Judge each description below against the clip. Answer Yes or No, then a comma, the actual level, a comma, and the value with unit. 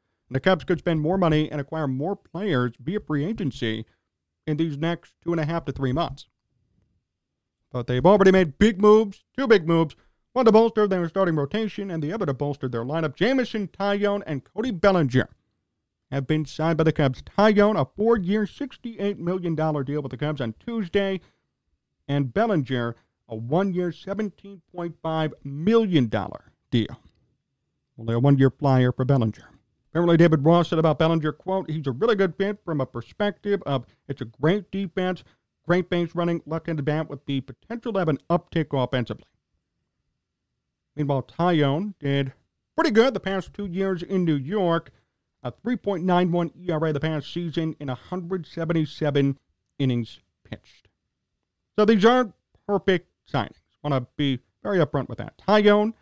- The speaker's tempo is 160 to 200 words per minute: Yes, average, 165 wpm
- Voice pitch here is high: No, medium, 160 Hz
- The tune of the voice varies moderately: No, wide, 6.0 semitones